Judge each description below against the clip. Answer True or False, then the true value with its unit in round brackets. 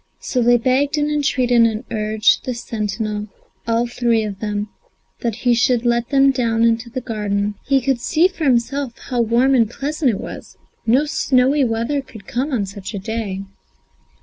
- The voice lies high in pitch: True (235 Hz)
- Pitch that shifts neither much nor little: True (3.2 semitones)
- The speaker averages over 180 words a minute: False (175 wpm)